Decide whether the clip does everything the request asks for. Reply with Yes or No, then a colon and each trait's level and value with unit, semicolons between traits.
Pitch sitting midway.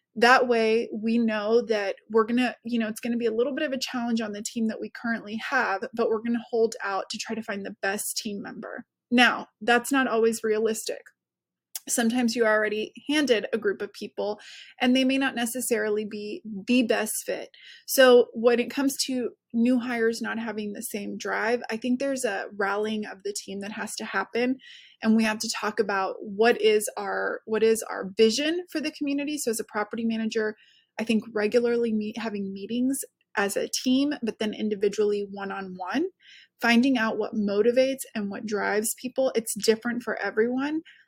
No: high, 230 Hz